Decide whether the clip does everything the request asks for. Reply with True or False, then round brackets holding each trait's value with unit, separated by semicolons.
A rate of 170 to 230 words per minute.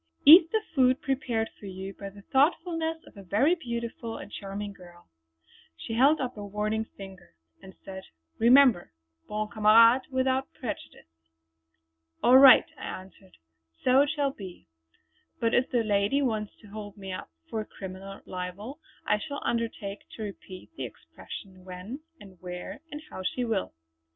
False (155 wpm)